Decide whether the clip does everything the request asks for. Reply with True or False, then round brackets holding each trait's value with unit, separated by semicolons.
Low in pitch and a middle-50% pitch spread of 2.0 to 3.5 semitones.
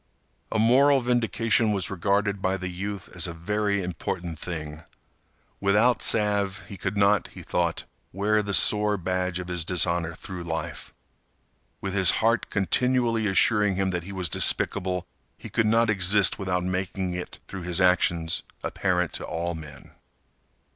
True (95 Hz; 2.9 semitones)